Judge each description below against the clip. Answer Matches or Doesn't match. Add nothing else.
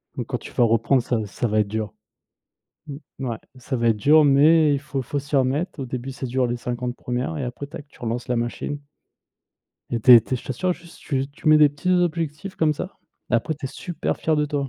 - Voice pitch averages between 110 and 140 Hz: Matches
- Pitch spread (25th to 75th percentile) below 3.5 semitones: Doesn't match